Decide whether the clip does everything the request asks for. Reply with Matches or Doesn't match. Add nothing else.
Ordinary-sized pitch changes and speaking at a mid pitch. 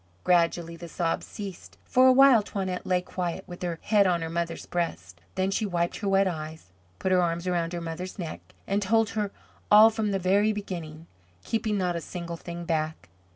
Matches